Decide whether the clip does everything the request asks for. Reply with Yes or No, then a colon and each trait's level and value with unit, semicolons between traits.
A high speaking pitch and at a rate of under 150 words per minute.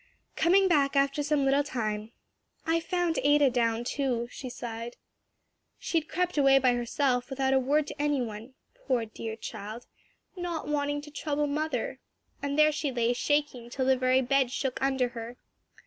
No: very high, 270 Hz; average, 170 wpm